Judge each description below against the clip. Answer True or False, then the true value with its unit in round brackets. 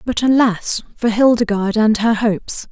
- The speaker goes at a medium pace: True (155 wpm)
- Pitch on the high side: True (220 Hz)